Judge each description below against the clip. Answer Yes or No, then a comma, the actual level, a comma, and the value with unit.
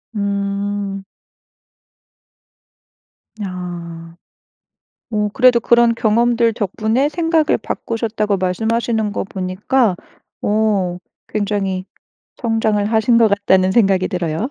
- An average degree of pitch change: Yes, average, 3.2 semitones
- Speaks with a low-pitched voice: No, high, 210 Hz